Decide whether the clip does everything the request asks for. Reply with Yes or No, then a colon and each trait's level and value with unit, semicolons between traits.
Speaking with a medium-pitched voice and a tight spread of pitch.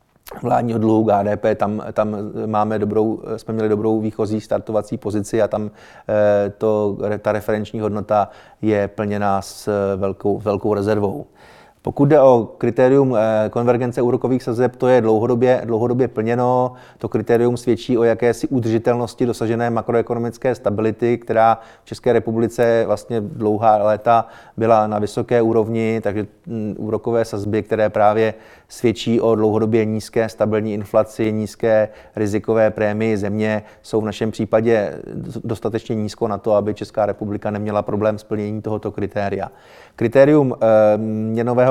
No: low, 110 Hz; narrow, 1.6 semitones